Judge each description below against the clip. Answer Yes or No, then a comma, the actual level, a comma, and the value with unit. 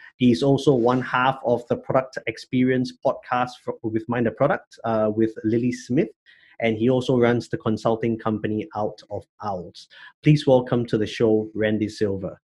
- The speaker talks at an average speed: Yes, average, 170 wpm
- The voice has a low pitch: Yes, low, 120 Hz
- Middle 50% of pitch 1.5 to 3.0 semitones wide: Yes, narrow, 2.4 semitones